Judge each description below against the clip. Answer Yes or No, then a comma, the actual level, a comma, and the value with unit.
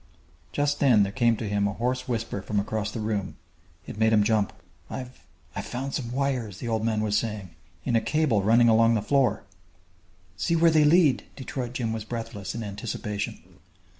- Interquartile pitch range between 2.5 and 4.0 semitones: Yes, average, 3.5 semitones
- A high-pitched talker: No, low, 115 Hz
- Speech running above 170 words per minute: Yes, average, 195 wpm